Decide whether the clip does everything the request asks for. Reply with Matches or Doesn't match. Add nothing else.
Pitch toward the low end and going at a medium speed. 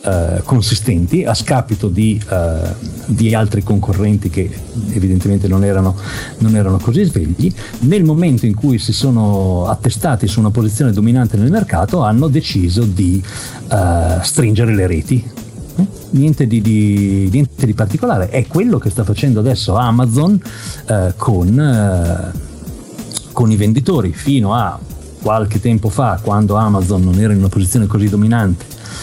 Matches